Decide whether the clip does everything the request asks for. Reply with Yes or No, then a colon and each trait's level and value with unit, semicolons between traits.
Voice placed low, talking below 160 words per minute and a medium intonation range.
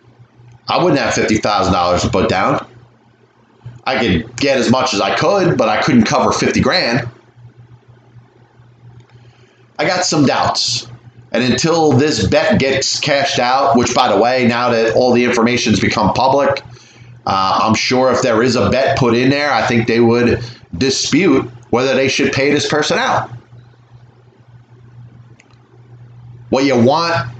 No: low, 120 Hz; average, 150 wpm; narrow, 1.4 semitones